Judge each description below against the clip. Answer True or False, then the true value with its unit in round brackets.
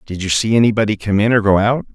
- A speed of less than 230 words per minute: False (275 wpm)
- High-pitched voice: False (105 Hz)